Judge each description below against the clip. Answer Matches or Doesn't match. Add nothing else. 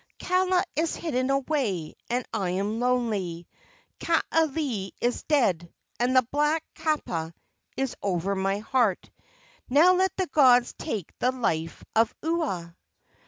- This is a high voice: Matches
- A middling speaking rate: Doesn't match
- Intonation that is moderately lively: Doesn't match